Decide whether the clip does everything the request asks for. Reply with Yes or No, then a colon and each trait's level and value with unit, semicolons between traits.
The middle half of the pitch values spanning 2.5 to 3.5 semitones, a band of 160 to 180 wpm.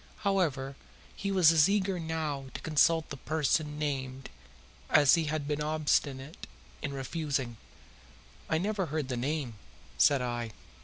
No: average, 3.2 semitones; average, 140 wpm